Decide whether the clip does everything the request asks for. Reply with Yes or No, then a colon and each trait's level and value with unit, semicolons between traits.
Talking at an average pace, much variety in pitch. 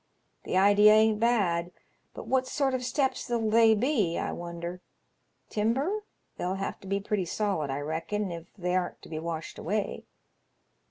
No: average, 165 wpm; average, 4.7 semitones